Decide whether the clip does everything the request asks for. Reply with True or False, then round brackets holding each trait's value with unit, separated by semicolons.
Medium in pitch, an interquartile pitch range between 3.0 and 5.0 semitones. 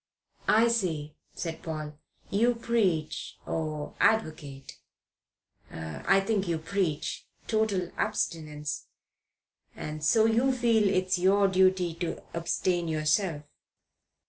True (175 Hz; 4.7 semitones)